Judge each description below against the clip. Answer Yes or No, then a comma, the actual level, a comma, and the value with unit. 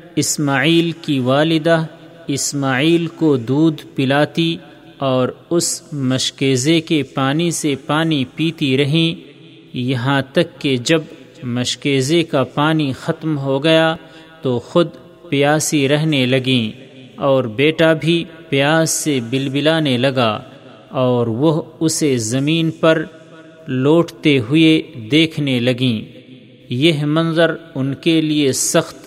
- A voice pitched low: No, medium, 150 Hz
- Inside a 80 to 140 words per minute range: Yes, slow, 110 wpm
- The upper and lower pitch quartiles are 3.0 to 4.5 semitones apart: Yes, average, 3.4 semitones